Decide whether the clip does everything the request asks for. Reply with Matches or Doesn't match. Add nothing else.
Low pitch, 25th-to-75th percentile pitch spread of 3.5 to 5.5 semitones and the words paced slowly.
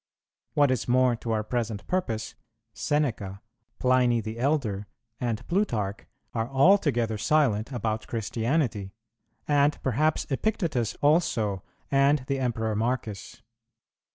Matches